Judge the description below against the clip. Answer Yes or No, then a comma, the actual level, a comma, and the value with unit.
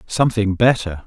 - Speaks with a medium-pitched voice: No, low, 105 Hz